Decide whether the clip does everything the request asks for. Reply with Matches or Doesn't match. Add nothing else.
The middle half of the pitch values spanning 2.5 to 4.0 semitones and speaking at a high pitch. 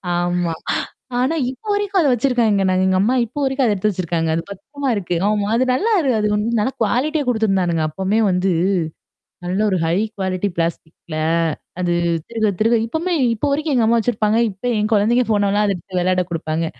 Doesn't match